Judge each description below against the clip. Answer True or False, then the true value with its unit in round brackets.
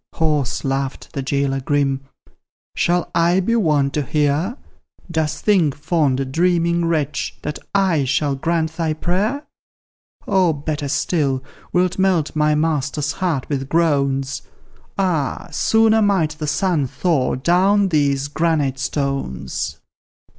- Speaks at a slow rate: True (125 wpm)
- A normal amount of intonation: True (3.9 semitones)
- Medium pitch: True (155 Hz)